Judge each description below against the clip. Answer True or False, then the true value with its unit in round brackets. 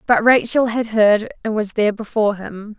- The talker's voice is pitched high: True (215 Hz)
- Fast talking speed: False (195 wpm)